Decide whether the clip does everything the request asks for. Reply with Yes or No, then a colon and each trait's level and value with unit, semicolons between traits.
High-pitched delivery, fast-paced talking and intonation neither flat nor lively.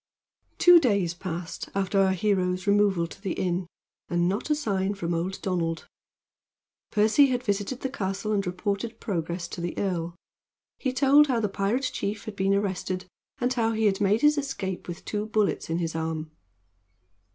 No: high, 195 Hz; average, 175 wpm; average, 3.6 semitones